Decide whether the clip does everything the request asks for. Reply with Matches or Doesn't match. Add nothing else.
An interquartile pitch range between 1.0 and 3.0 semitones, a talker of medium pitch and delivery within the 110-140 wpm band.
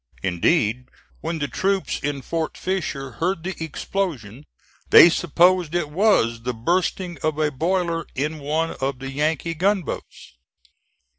Doesn't match